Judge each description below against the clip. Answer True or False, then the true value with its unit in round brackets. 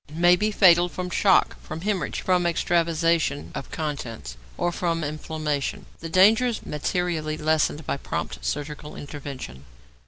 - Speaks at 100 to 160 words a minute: True (145 wpm)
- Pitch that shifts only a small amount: False (3.3 semitones)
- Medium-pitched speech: True (160 Hz)